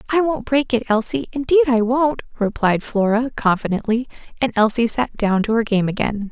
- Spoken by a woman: Yes, female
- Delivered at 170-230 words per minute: Yes, average, 180 wpm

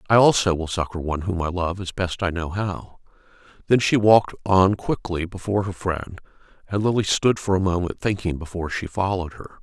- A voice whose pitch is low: Yes, very low, 90 Hz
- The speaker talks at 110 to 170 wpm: No, average, 200 wpm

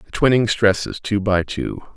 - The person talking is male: Yes, male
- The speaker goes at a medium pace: Yes, average, 185 wpm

